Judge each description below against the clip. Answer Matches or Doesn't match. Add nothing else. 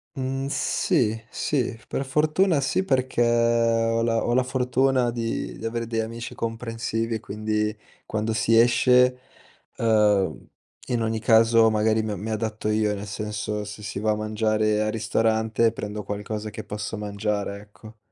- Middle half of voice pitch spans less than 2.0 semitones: Matches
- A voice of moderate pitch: Doesn't match